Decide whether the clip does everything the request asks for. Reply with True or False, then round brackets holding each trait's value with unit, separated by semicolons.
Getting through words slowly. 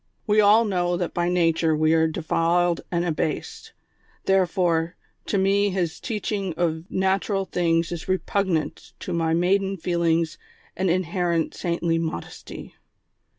True (130 wpm)